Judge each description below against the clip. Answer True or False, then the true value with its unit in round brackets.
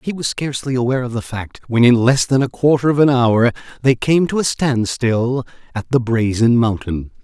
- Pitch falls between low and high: False (125 Hz)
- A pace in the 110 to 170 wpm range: False (200 wpm)